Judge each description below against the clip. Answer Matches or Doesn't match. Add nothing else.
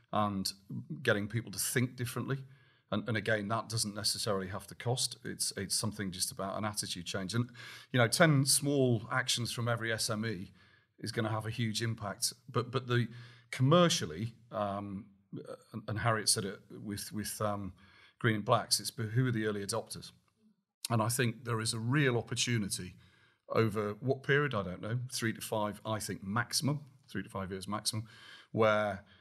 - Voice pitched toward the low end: Matches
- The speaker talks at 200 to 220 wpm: Doesn't match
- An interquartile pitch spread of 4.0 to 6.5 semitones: Doesn't match